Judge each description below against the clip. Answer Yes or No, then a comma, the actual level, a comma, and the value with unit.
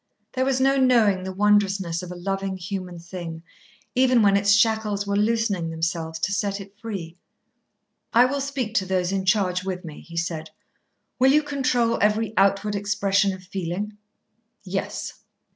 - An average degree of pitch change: Yes, average, 3.3 semitones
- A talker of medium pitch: No, high, 200 Hz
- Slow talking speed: No, average, 160 wpm